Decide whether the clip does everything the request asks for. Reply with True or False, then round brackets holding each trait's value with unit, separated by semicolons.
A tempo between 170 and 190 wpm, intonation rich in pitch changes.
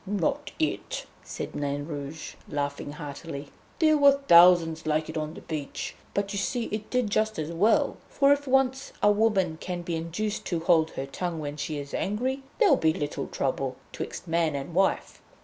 True (185 wpm; 5.8 semitones)